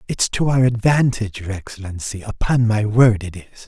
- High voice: No, low, 110 Hz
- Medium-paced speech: Yes, average, 180 wpm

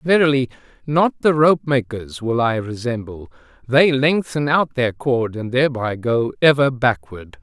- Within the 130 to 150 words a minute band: Yes, average, 145 wpm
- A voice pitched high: No, low, 130 Hz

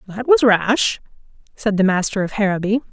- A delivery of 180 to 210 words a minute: No, average, 165 wpm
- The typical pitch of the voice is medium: No, high, 215 Hz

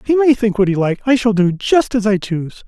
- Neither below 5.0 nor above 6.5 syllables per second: Yes, 6.0 syllables/s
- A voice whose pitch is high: Yes, high, 215 Hz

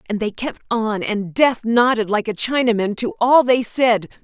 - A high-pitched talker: Yes, high, 225 Hz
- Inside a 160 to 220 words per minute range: Yes, average, 200 wpm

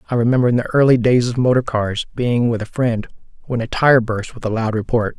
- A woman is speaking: No, male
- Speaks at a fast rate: Yes, fast, 245 wpm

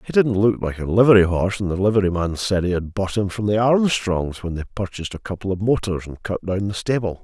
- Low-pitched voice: Yes, low, 100 Hz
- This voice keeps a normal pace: No, fast, 250 wpm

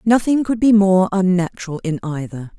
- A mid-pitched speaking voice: No, high, 195 Hz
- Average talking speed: Yes, average, 165 wpm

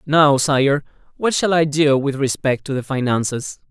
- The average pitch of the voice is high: No, medium, 145 Hz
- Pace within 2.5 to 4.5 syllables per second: Yes, 4.4 syllables/s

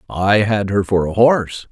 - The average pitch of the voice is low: Yes, low, 105 Hz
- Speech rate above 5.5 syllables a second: No, 4.6 syllables/s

